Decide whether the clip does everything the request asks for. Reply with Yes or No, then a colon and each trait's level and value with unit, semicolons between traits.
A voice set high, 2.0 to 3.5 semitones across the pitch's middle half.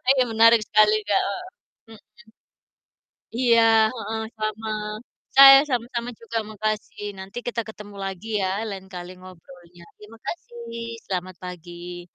No: high, 210 Hz; average, 3.9 semitones